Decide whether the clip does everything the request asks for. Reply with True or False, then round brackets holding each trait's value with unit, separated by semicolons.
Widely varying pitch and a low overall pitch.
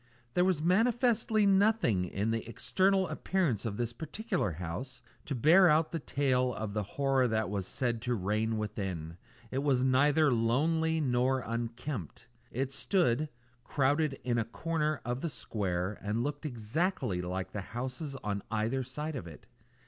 True (6.0 semitones; 125 Hz)